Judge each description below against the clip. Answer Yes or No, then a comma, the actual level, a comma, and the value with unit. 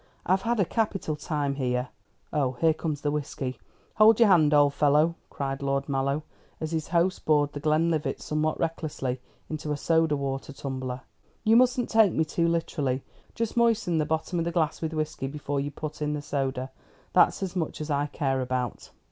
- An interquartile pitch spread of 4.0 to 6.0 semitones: No, average, 3.2 semitones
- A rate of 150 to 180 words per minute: No, average, 190 wpm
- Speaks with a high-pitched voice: No, medium, 150 Hz